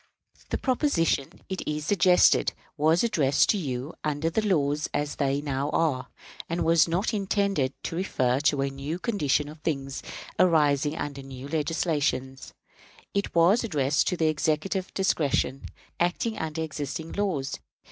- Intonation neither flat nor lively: Yes, average, 4.0 semitones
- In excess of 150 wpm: No, average, 145 wpm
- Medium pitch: Yes, medium, 155 Hz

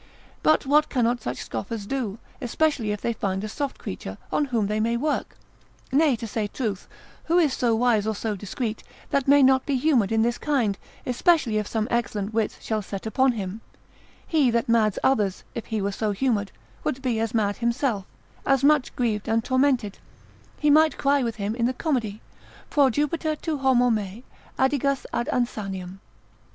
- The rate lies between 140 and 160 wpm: No, average, 185 wpm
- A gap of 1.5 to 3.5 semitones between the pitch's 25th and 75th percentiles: No, average, 4.2 semitones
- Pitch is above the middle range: Yes, high, 235 Hz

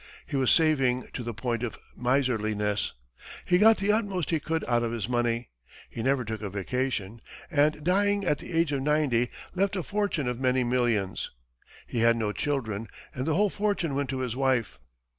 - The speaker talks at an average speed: Yes, average, 190 wpm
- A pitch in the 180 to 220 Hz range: No, low, 130 Hz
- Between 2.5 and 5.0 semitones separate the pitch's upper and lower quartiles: No, wide, 5.4 semitones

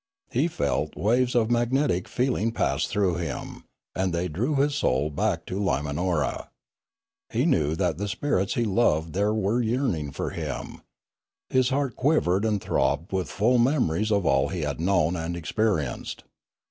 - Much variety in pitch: Yes, wide, 6.6 semitones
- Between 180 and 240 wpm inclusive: No, average, 160 wpm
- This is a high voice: No, low, 100 Hz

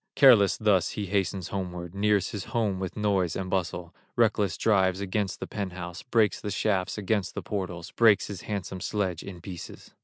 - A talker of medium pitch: No, very low, 95 Hz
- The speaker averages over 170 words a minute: Yes, average, 180 wpm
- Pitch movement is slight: Yes, narrow, 2.3 semitones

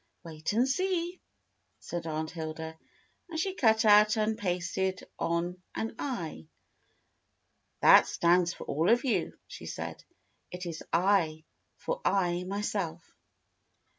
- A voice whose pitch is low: No, medium, 180 Hz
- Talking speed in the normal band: No, slow, 125 wpm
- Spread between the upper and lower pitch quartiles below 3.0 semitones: No, average, 4.9 semitones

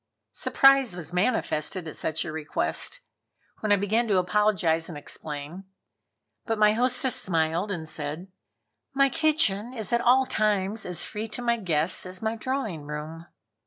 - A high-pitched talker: Yes, high, 195 Hz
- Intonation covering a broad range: Yes, wide, 5.8 semitones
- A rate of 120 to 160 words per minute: Yes, average, 155 wpm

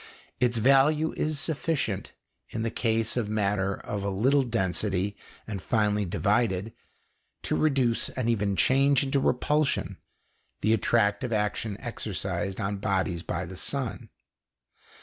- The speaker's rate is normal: No, slow, 125 wpm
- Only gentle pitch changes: No, average, 4.4 semitones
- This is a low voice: Yes, low, 110 Hz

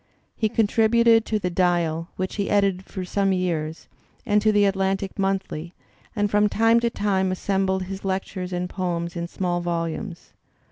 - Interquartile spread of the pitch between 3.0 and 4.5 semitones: No, narrow, 2.5 semitones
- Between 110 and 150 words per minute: No, average, 170 wpm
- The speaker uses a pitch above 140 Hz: Yes, high, 190 Hz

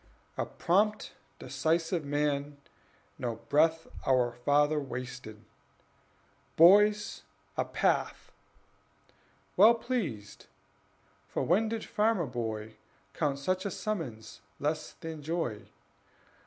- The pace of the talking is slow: Yes, slow, 95 wpm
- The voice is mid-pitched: Yes, medium, 150 Hz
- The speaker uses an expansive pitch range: Yes, wide, 6.5 semitones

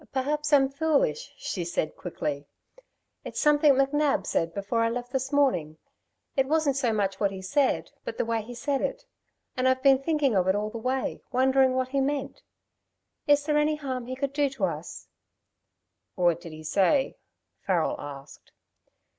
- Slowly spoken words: No, average, 170 wpm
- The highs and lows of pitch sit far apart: Yes, wide, 6.3 semitones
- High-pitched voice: Yes, very high, 260 Hz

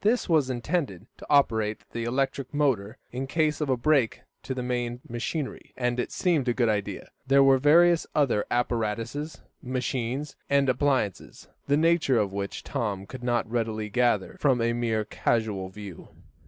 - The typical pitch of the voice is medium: No, low, 125 Hz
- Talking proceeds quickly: No, average, 165 wpm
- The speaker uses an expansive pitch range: No, average, 4.0 semitones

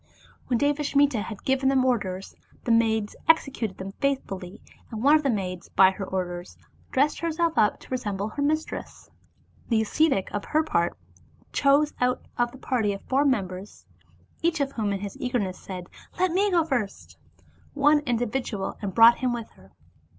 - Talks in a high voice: Yes, high, 240 Hz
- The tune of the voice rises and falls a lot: Yes, wide, 6.3 semitones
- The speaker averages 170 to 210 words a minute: Yes, average, 190 wpm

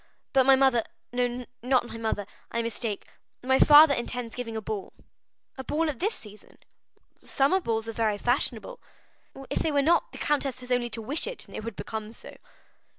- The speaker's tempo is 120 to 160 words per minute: No, average, 175 wpm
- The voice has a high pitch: Yes, high, 245 Hz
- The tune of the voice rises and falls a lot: No, average, 3.5 semitones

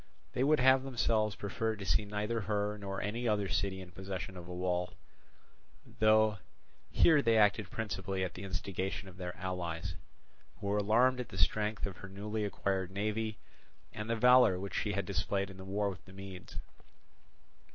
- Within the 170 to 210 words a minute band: Yes, average, 180 wpm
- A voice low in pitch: Yes, low, 100 Hz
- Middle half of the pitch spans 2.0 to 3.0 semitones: Yes, narrow, 2.4 semitones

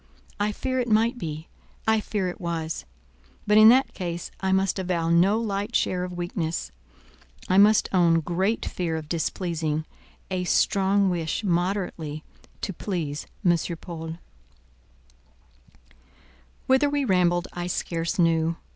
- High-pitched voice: No, medium, 180 Hz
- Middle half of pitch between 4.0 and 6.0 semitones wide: No, average, 3.5 semitones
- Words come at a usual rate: No, slow, 130 wpm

